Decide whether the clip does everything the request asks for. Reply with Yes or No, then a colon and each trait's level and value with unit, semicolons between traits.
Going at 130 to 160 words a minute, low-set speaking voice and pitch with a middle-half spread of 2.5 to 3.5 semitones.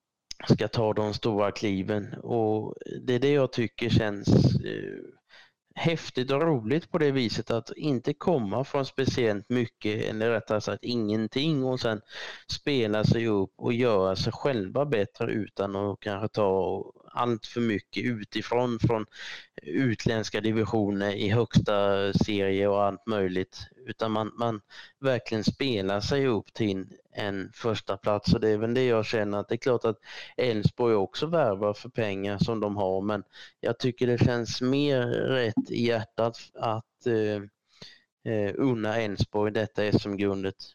Yes: average, 150 wpm; low, 110 Hz; average, 2.8 semitones